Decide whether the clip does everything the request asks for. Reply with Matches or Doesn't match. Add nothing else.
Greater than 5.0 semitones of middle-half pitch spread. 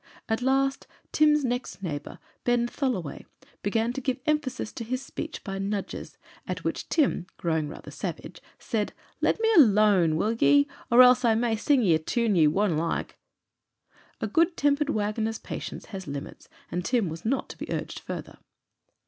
Matches